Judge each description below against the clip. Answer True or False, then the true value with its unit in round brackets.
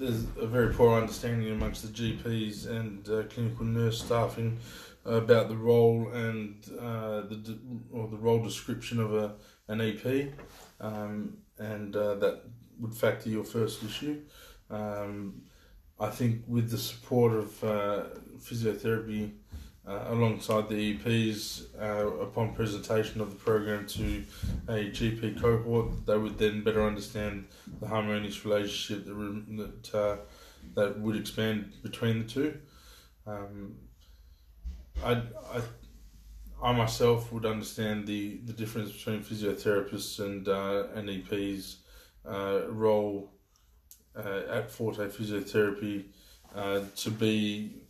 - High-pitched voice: False (110 Hz)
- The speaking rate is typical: False (125 wpm)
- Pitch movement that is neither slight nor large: False (1.9 semitones)